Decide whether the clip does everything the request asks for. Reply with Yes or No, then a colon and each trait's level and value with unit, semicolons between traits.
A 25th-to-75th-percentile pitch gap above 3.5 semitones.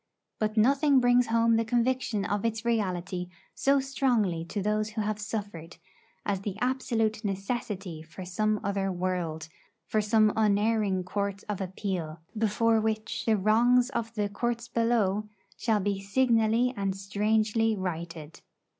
No: average, 2.9 semitones